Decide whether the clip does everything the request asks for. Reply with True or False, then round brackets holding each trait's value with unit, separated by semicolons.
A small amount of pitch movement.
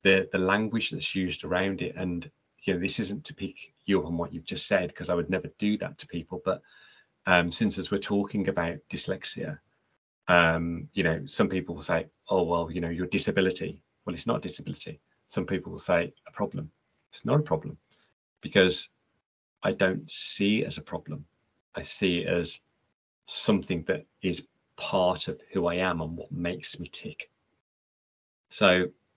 True (2.2 semitones)